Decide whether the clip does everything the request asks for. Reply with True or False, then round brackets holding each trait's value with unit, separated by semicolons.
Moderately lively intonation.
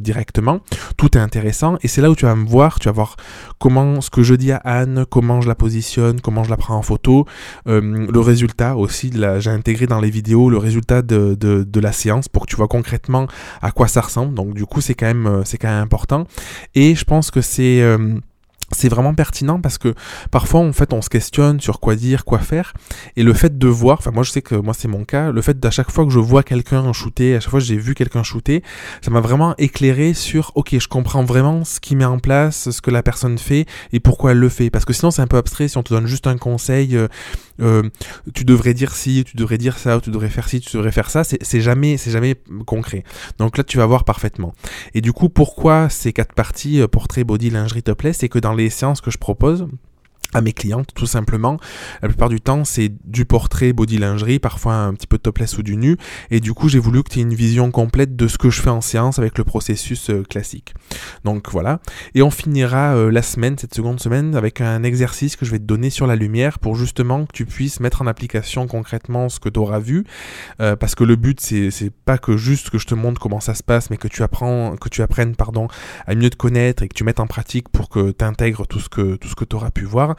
True (3.1 semitones)